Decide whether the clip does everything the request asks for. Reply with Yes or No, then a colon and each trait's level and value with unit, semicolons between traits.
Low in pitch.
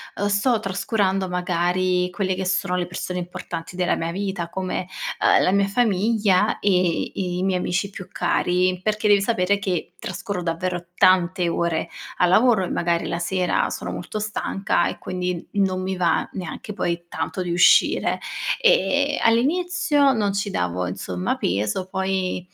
No: medium, 185 Hz